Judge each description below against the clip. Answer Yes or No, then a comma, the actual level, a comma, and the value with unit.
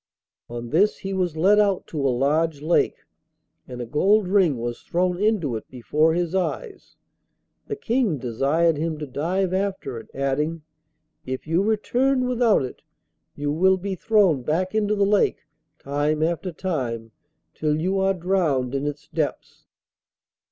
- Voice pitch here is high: No, medium, 165 Hz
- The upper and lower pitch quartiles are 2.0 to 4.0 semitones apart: No, average, 5.3 semitones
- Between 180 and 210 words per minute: No, average, 155 wpm